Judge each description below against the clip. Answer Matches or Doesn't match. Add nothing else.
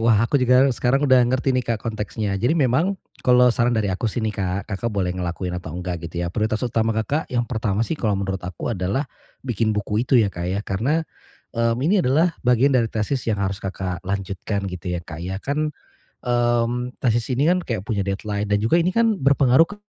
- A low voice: Matches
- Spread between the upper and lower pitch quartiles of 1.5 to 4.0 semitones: Doesn't match